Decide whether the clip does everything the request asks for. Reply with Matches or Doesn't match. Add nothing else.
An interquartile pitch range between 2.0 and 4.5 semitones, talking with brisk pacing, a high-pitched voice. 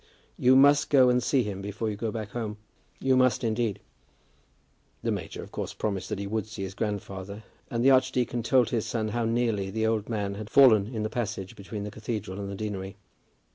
Doesn't match